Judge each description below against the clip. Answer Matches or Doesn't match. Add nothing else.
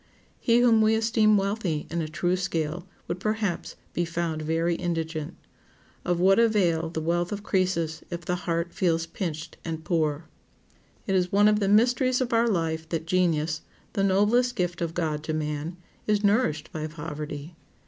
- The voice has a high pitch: Doesn't match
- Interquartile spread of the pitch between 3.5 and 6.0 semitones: Matches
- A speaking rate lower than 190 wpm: Matches